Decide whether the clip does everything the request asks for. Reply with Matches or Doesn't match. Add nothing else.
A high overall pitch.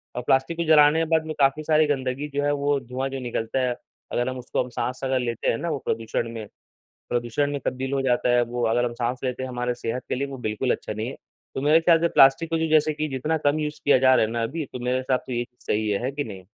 Doesn't match